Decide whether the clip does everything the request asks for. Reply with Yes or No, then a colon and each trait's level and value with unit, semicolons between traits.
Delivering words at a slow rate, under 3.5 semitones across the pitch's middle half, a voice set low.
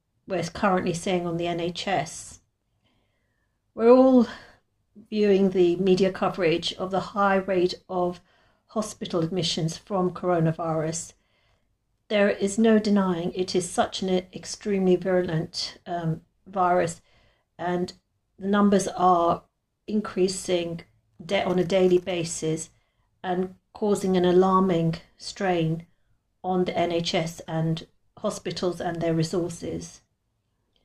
No: slow, 110 wpm; average, 2.7 semitones; medium, 180 Hz